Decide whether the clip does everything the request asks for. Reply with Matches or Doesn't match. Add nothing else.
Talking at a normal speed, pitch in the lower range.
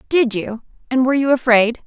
Doesn't match